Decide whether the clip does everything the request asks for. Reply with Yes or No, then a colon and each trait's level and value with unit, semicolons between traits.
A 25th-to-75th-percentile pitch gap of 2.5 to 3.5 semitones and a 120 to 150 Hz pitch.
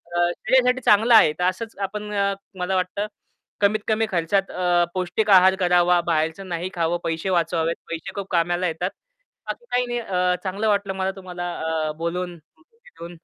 No: average, 2.8 semitones; medium, 185 Hz